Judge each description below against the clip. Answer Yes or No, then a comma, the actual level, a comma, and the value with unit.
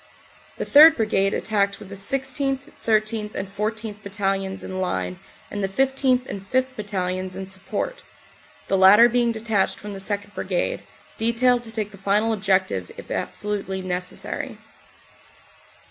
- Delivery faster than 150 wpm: No, average, 145 wpm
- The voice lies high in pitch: Yes, high, 205 Hz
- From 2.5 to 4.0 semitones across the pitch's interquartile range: Yes, average, 3.2 semitones